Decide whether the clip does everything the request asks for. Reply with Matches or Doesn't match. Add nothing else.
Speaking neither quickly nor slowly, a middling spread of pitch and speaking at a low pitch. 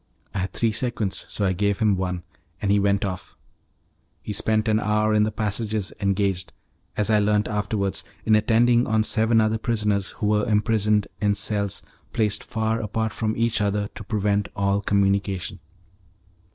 Doesn't match